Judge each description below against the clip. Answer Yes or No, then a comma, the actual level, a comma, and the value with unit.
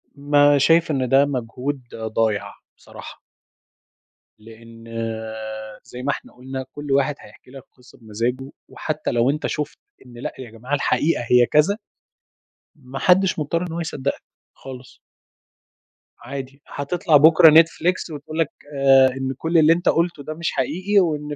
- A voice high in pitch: No, medium, 140 Hz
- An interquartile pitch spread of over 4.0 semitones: No, average, 3.7 semitones